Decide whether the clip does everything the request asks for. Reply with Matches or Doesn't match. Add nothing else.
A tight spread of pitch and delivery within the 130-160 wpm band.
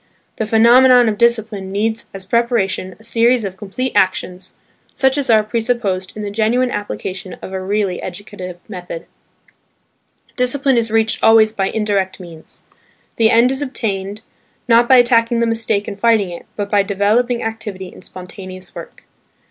Doesn't match